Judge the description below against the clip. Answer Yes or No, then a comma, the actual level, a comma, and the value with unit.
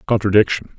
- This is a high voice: No, low, 105 Hz